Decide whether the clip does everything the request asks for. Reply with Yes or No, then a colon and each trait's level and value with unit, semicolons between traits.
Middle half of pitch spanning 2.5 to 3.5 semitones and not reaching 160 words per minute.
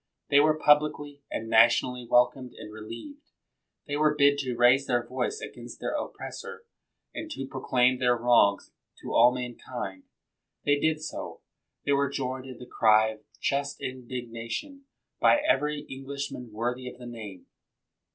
Yes: average, 3.2 semitones; average, 150 wpm